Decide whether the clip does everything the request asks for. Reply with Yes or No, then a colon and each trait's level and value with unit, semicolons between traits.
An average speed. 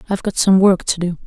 No: fast, 285 wpm